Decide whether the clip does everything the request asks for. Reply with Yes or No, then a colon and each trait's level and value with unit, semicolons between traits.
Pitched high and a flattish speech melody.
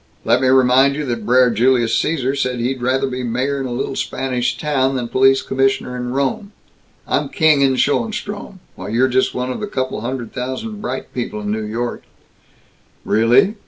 No: low, 130 Hz; narrow, 2.0 semitones